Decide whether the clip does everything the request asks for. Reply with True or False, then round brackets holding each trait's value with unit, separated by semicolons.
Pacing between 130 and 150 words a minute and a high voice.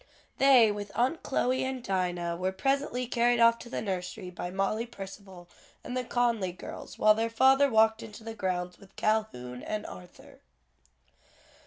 False (160 wpm; 215 Hz)